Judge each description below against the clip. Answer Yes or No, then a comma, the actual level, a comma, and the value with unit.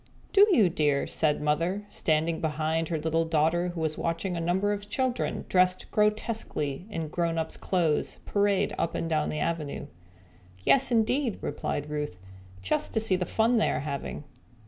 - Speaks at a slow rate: No, average, 165 wpm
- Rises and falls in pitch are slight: No, average, 4.8 semitones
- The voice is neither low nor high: Yes, medium, 170 Hz